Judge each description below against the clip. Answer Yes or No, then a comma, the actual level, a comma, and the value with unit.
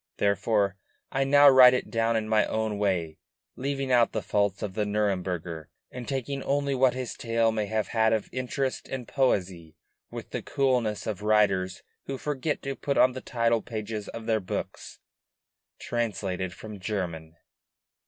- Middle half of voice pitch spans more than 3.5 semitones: Yes, average, 4.1 semitones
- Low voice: Yes, low, 110 Hz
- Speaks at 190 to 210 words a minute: No, average, 165 wpm